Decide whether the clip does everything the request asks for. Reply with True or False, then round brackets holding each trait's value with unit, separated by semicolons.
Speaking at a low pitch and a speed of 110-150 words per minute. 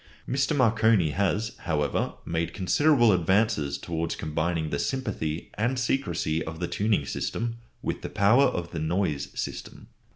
True (95 Hz; 140 wpm)